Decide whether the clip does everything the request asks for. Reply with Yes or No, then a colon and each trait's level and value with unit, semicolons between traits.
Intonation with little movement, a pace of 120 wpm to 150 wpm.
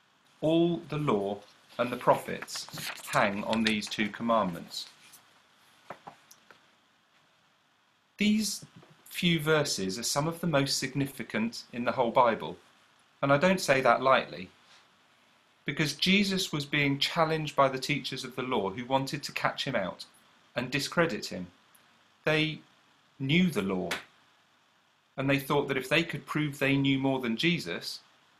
No: average, 3.6 semitones; average, 140 wpm